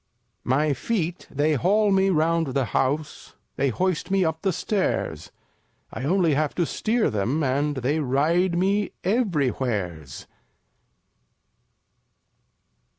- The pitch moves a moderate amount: No, wide, 5.7 semitones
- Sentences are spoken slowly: Yes, slow, 120 wpm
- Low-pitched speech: No, medium, 155 Hz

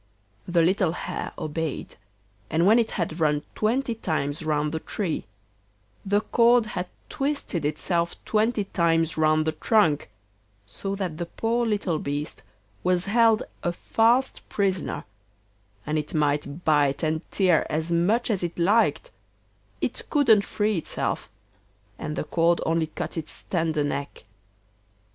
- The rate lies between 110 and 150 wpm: Yes, average, 140 wpm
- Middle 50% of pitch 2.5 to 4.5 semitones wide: No, average, 5.2 semitones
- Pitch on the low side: No, medium, 170 Hz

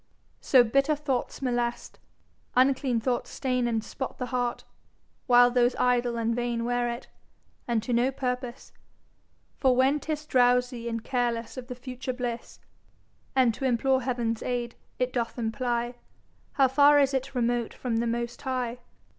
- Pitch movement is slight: Yes, narrow, 1.6 semitones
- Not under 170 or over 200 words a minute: No, average, 155 wpm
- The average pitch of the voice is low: No, high, 245 Hz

